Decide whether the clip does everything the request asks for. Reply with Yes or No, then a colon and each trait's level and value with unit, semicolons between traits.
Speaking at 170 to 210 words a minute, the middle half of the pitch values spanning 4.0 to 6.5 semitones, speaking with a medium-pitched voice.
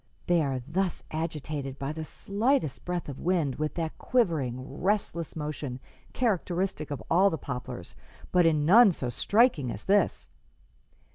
No: average, 145 wpm; average, 5.0 semitones; medium, 160 Hz